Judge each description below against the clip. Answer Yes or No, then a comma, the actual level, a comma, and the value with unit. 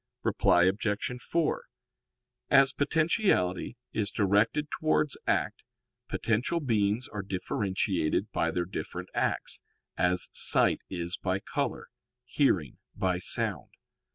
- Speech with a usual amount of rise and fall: No, wide, 6.7 semitones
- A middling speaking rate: No, slow, 105 wpm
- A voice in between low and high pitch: No, low, 105 Hz